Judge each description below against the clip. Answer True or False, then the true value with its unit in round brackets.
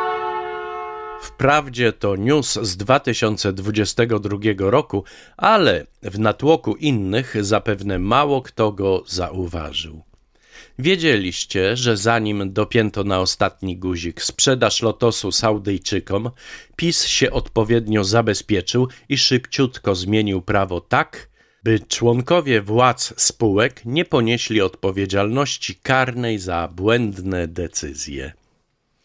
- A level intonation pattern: False (4.0 semitones)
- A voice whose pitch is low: True (105 Hz)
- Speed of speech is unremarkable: False (95 wpm)